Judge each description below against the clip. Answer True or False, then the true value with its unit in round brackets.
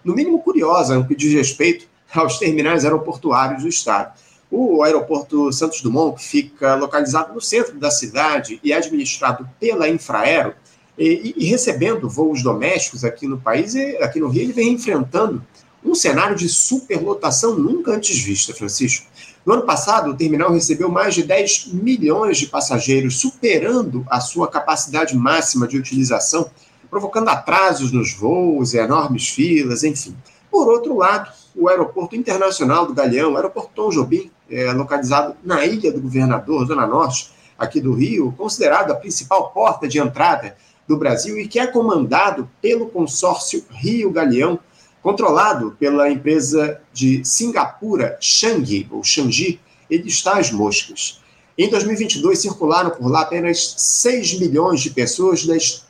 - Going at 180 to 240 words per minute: False (145 wpm)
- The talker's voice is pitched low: False (165 Hz)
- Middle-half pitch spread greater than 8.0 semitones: True (8.8 semitones)